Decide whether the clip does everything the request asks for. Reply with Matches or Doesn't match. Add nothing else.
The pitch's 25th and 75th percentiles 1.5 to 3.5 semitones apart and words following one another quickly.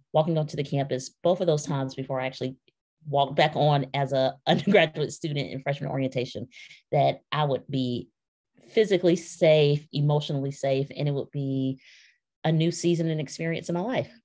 Doesn't match